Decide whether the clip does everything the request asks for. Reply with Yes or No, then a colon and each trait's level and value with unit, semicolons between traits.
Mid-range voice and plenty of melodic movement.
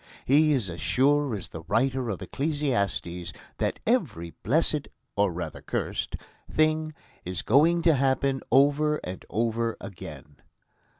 No: low, 130 Hz; wide, 7.5 semitones